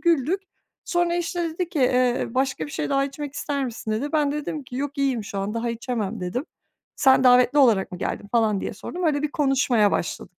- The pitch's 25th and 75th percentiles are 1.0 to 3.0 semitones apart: No, average, 4.4 semitones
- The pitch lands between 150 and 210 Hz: No, very high, 265 Hz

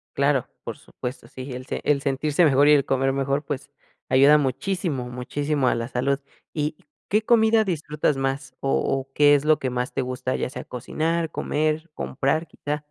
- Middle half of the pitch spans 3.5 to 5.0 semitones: No, narrow, 2.5 semitones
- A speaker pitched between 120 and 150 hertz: Yes, medium, 140 Hz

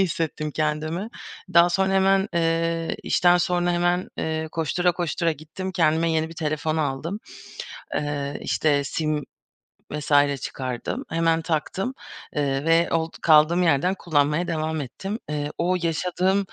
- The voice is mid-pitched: Yes, medium, 165 Hz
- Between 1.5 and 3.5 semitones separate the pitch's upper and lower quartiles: Yes, average, 2.7 semitones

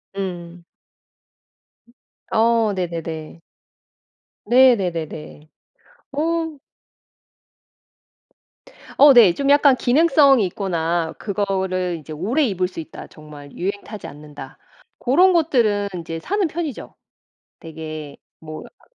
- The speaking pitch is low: No, high, 190 Hz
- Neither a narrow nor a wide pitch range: No, wide, 8.2 semitones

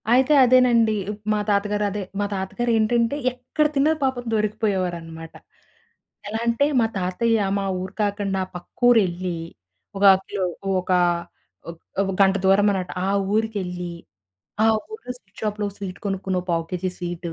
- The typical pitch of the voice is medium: No, high, 205 Hz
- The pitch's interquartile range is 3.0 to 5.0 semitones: Yes, average, 3.7 semitones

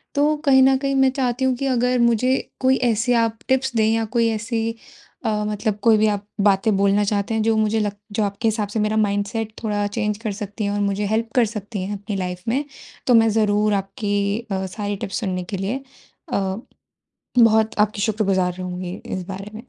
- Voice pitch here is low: No, high, 215 Hz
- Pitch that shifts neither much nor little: No, narrow, 2.2 semitones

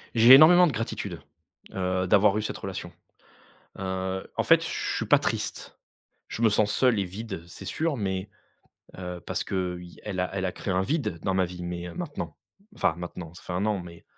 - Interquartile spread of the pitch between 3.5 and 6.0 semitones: No, average, 3.0 semitones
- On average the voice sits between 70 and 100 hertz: Yes, very low, 95 Hz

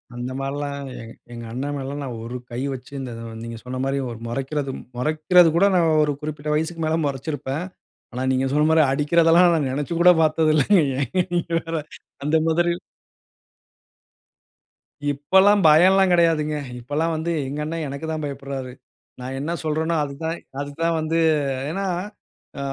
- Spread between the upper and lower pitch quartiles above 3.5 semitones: No, average, 3.2 semitones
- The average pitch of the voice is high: No, medium, 150 Hz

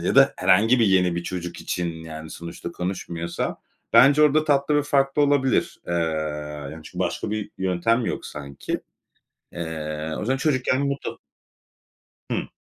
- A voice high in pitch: No, very low, 95 Hz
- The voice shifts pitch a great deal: Yes, wide, 8.2 semitones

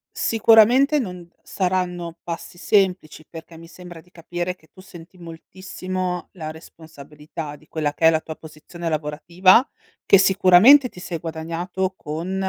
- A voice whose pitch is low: No, medium, 175 Hz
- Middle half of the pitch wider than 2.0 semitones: Yes, narrow, 2.6 semitones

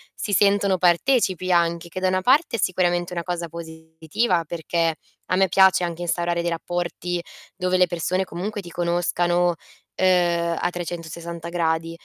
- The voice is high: No, medium, 175 Hz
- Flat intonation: Yes, narrow, 1.5 semitones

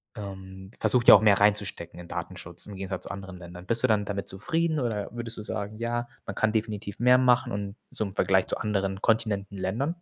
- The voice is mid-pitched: No, low, 105 Hz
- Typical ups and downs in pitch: Yes, average, 3.1 semitones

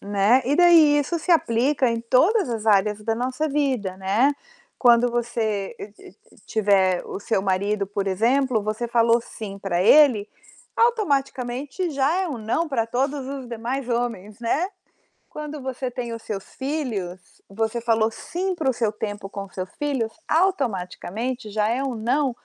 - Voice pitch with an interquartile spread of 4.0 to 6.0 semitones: Yes, average, 4.7 semitones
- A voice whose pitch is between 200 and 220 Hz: No, high, 235 Hz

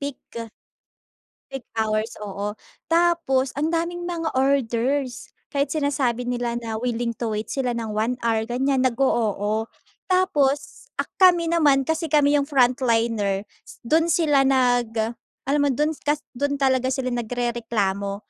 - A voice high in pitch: Yes, very high, 260 Hz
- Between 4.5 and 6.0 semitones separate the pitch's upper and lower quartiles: No, average, 3.9 semitones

